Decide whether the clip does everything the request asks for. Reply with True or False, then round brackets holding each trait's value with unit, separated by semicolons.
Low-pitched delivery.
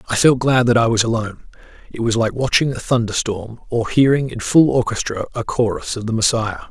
True (115 Hz)